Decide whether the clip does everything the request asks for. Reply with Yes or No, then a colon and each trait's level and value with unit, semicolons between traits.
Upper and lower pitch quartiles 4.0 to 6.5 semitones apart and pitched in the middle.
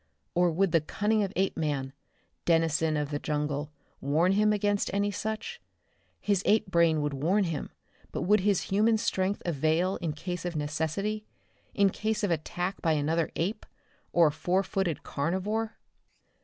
Yes: average, 4.5 semitones; medium, 175 Hz